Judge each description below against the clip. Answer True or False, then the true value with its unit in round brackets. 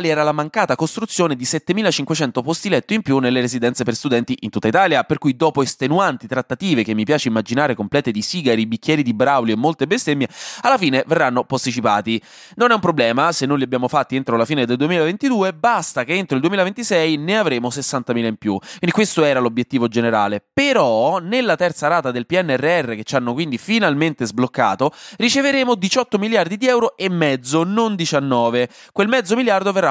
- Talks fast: True (185 wpm)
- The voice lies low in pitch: False (150 Hz)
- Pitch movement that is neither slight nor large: False (7.3 semitones)